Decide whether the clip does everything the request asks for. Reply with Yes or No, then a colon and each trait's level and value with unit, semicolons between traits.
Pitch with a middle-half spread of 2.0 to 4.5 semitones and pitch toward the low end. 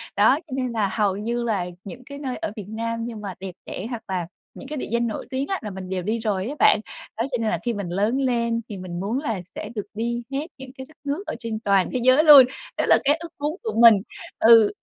No: average, 4.2 semitones; high, 230 Hz